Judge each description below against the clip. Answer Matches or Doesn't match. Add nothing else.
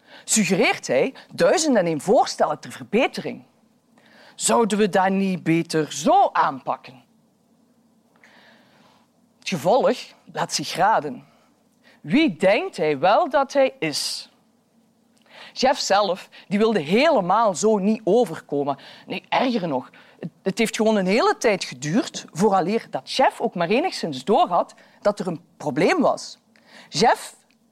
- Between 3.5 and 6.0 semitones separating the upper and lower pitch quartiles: Matches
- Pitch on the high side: Matches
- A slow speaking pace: Matches